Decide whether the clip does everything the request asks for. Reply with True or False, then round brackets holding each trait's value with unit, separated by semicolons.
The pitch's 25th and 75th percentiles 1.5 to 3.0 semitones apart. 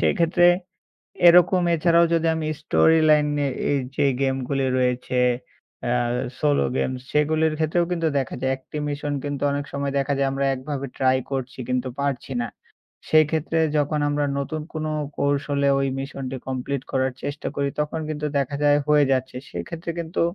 True (2.5 semitones)